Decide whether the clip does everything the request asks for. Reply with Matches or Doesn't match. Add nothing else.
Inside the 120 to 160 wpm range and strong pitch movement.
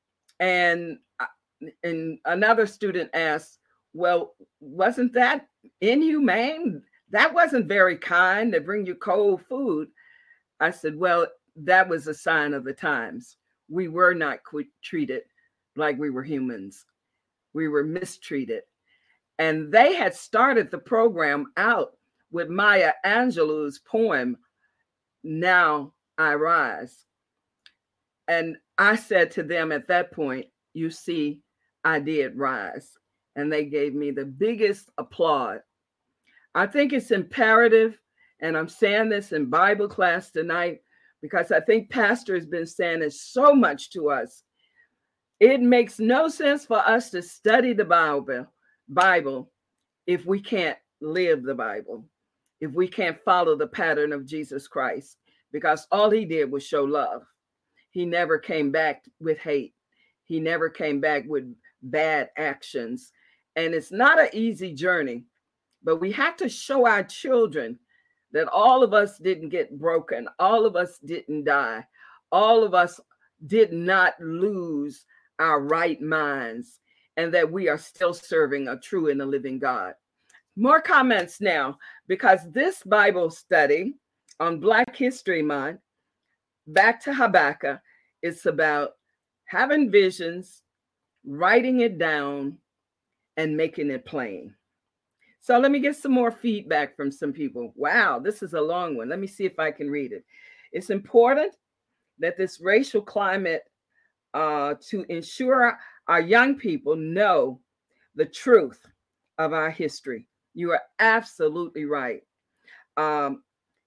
Matches